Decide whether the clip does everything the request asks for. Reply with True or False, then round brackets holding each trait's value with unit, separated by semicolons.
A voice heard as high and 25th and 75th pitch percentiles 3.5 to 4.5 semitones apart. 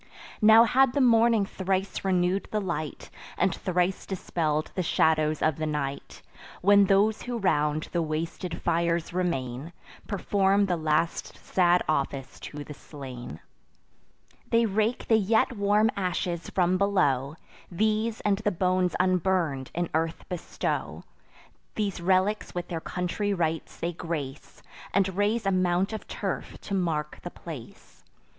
False (180 Hz; 4.0 semitones)